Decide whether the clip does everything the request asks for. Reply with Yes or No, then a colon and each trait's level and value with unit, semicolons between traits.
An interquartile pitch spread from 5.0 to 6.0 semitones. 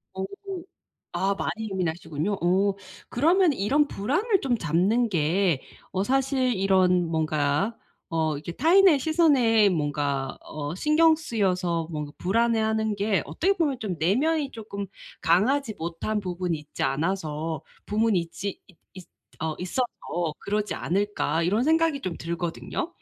No: wide, 6.8 semitones